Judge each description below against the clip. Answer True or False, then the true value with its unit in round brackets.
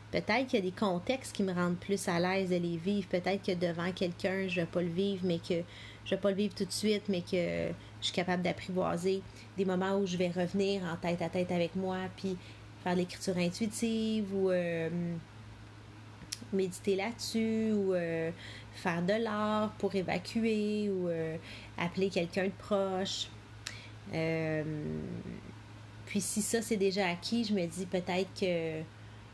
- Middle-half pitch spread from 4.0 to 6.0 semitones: False (3.3 semitones)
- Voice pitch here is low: False (180 Hz)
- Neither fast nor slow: True (175 wpm)